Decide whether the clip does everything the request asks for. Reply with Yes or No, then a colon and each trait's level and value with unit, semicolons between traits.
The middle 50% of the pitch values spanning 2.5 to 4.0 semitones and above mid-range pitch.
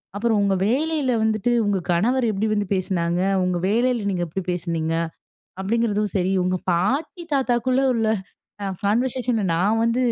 No: average, 4.5 semitones; high, 215 Hz